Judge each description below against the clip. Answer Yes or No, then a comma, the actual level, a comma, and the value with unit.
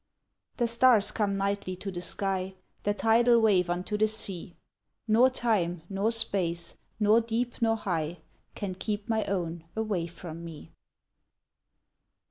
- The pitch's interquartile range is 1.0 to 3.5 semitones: No, average, 3.9 semitones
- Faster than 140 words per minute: No, slow, 135 wpm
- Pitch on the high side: Yes, high, 200 Hz